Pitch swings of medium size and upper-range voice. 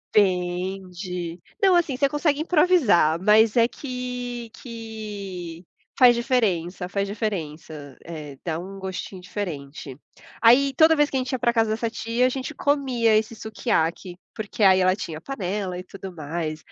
No: wide, 5.8 semitones; high, 205 Hz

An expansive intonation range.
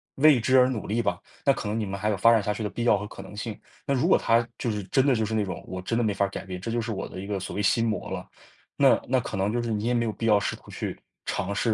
No: average, 2.7 semitones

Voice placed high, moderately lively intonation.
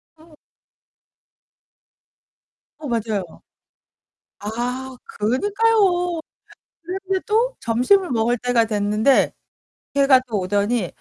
No: very high, 250 Hz; wide, 8.2 semitones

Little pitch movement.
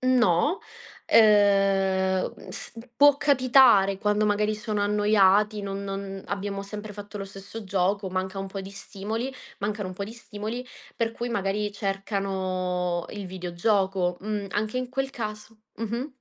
Yes: narrow, 1.9 semitones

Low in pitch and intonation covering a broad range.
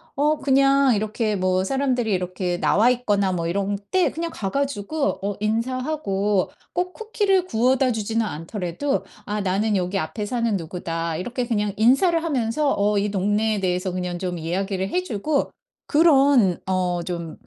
No: high, 210 Hz; wide, 6.3 semitones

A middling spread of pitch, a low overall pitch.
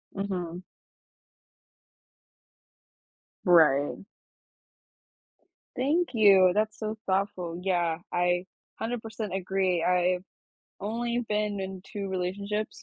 No: average, 3.0 semitones; high, 190 Hz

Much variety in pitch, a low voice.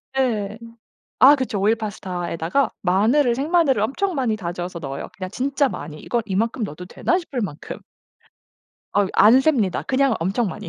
No: wide, 6.2 semitones; high, 215 Hz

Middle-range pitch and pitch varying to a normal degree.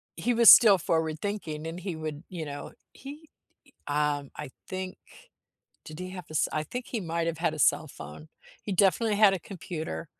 Yes: medium, 170 Hz; average, 4.1 semitones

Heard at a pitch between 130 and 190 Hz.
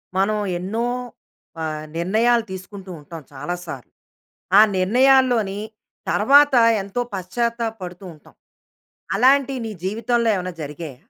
No: high, 200 Hz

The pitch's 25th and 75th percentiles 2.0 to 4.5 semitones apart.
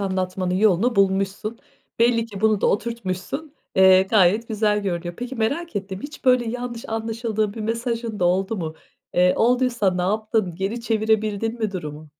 Yes: average, 3.5 semitones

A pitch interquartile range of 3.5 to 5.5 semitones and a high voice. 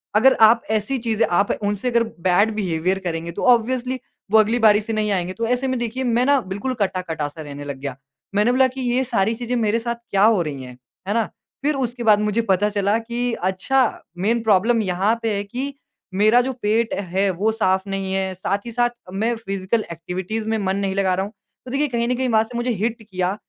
Yes: average, 3.8 semitones; high, 215 Hz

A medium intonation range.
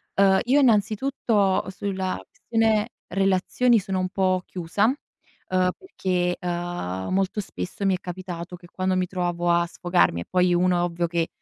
No: narrow, 2.1 semitones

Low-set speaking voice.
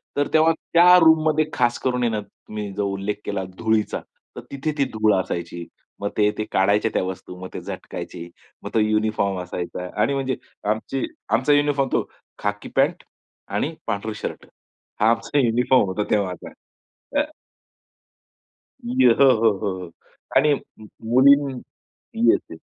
Yes: low, 110 Hz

